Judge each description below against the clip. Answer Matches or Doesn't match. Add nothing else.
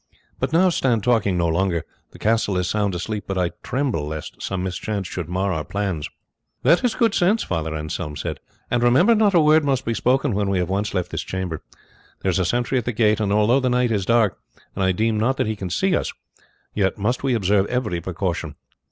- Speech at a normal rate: Doesn't match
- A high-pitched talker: Doesn't match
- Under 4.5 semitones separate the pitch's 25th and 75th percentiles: Doesn't match